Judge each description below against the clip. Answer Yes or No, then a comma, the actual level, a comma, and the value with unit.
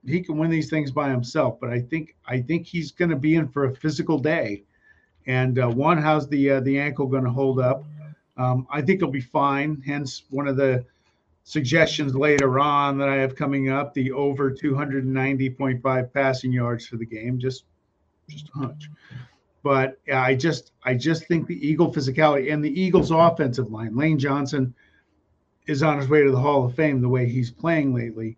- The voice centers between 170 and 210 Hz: No, medium, 140 Hz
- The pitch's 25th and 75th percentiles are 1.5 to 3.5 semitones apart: Yes, average, 2.9 semitones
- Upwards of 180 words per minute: Yes, average, 195 wpm